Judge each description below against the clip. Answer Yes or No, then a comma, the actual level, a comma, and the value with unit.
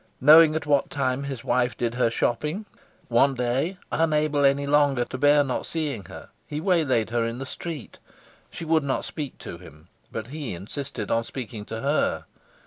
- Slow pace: No, average, 180 wpm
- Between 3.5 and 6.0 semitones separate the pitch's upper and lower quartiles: Yes, average, 3.9 semitones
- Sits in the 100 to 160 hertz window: Yes, medium, 140 Hz